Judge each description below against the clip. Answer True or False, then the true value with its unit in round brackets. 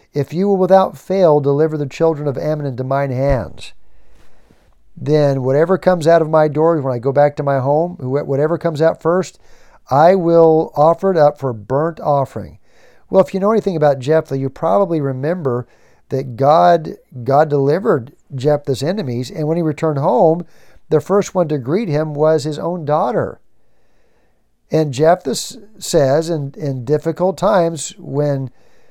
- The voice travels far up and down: False (3.3 semitones)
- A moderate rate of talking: True (160 wpm)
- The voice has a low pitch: False (150 Hz)